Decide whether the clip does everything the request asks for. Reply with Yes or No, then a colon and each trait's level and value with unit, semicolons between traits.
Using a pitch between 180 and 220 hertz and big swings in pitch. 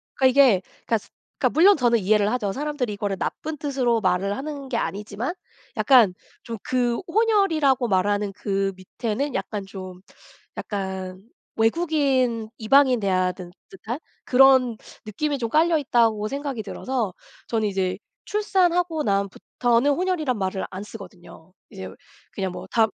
No: high, 230 Hz; wide, 6.0 semitones